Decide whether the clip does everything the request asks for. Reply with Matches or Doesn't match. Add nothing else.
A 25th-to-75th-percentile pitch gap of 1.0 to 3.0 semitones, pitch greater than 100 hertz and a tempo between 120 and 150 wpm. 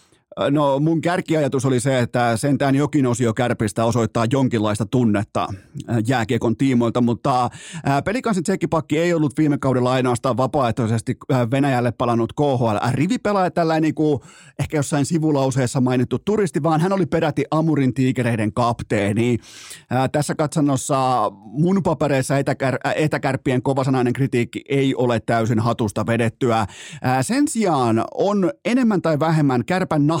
Doesn't match